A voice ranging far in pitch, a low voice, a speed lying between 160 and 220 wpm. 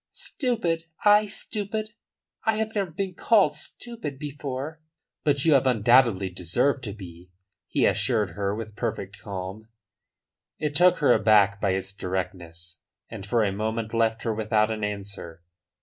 No: wide, 7.9 semitones; low, 115 Hz; average, 150 wpm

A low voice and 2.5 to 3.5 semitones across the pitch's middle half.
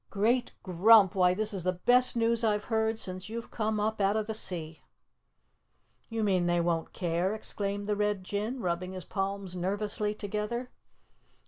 No: high, 205 Hz; average, 3.0 semitones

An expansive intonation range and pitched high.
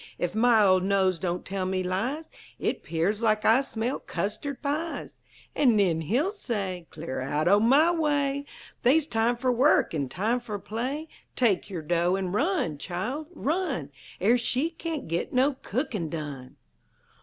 Yes: wide, 7.3 semitones; high, 220 Hz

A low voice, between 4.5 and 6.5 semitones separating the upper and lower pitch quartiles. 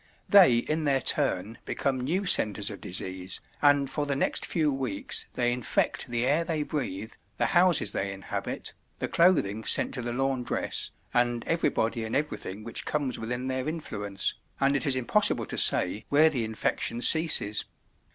Yes: low, 130 Hz; average, 5.2 semitones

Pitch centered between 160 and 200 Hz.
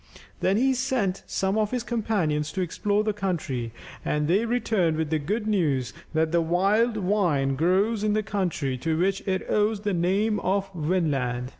Yes: high, 190 Hz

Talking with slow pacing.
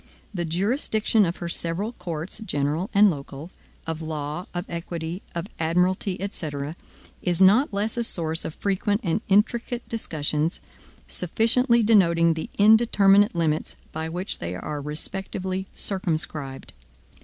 Yes: slow, 130 wpm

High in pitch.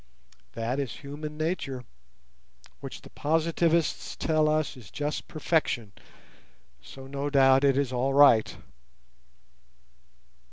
No: medium, 140 Hz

